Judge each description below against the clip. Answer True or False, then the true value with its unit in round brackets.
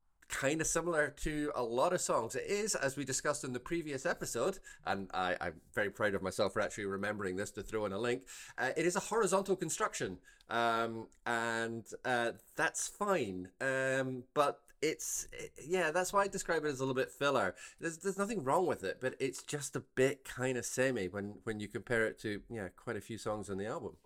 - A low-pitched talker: True (130 Hz)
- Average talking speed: False (215 wpm)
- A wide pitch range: True (7.0 semitones)